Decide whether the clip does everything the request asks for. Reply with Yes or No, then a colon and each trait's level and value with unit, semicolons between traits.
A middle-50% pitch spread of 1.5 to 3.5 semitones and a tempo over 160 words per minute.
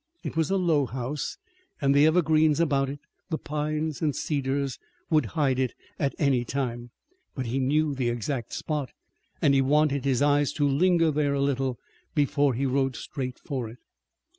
Yes: narrow, 2.4 semitones; average, 175 wpm